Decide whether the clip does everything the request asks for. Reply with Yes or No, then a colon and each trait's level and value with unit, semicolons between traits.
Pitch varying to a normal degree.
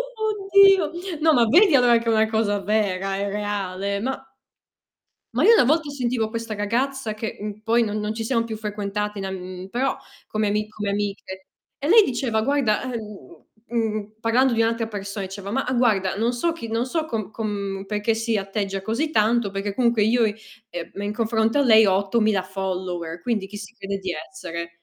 Yes: average, 3.1 semitones